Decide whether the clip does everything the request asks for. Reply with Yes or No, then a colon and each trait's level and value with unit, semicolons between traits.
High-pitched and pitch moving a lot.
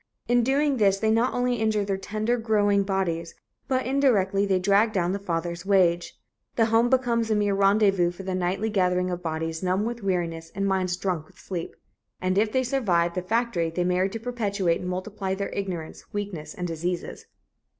No: high, 195 Hz; average, 3.6 semitones